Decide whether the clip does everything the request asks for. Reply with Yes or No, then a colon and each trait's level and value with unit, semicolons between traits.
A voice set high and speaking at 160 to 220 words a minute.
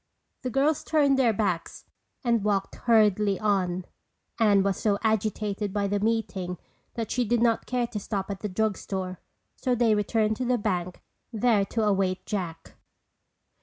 Yes: high, 210 Hz; average, 165 wpm